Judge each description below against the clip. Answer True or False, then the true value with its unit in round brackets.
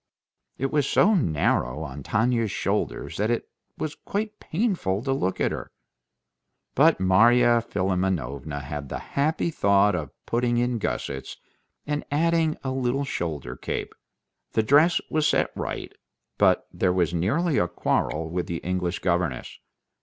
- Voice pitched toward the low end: True (110 Hz)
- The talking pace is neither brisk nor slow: True (145 wpm)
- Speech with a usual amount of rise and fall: False (8.3 semitones)